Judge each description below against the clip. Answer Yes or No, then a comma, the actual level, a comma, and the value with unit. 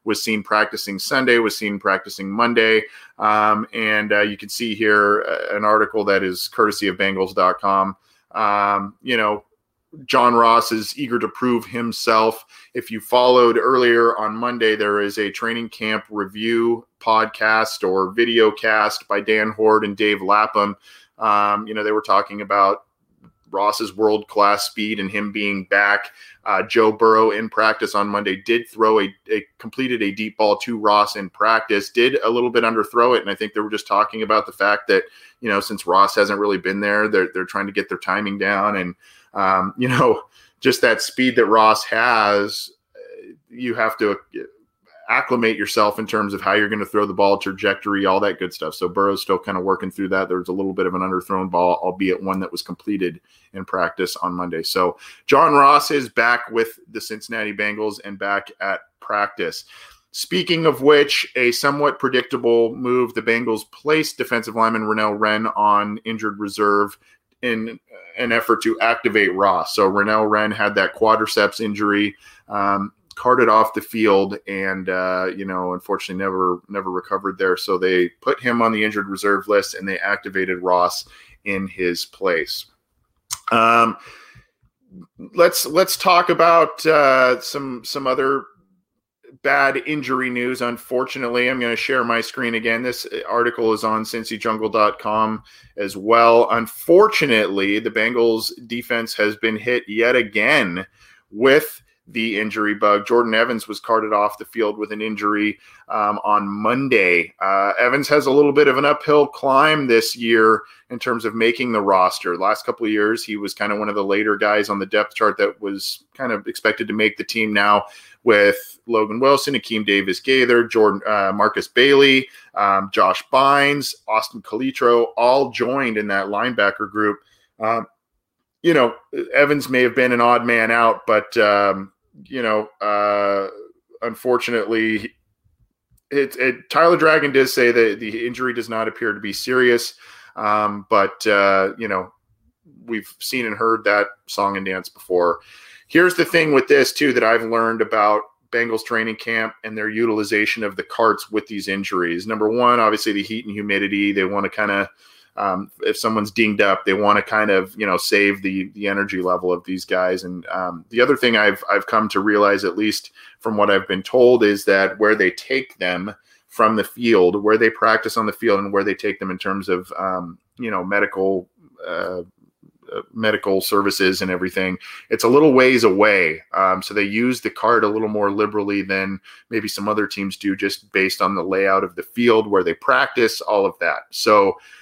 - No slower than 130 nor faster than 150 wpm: No, average, 180 wpm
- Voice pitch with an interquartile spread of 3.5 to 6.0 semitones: No, average, 2.7 semitones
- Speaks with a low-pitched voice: Yes, low, 105 Hz